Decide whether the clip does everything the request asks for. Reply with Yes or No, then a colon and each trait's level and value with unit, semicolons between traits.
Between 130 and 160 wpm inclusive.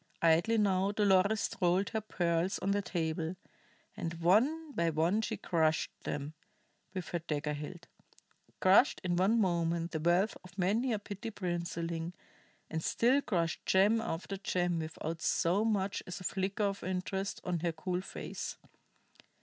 Yes: average, 150 wpm